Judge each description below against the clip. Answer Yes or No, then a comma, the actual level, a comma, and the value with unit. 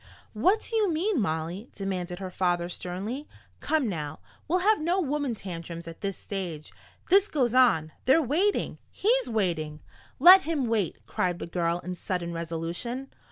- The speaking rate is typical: Yes, average, 160 wpm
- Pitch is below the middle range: No, high, 200 Hz